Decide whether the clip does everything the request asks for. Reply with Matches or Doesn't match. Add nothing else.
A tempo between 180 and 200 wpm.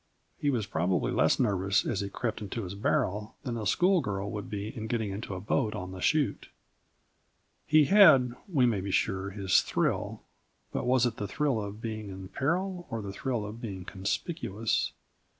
Matches